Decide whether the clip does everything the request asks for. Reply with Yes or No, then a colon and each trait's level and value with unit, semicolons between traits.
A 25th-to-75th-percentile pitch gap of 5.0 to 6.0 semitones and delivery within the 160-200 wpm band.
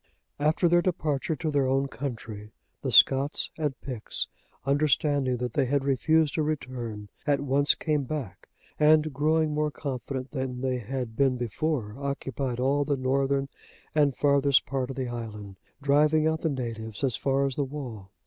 No: average, 2.8 semitones; average, 165 wpm